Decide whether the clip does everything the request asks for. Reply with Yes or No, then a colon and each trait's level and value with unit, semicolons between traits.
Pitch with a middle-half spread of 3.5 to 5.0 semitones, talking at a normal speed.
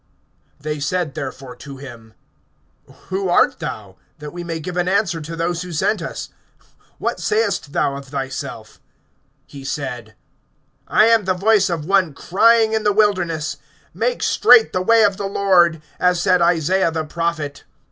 Yes: average, 4.5 semitones; average, 160 wpm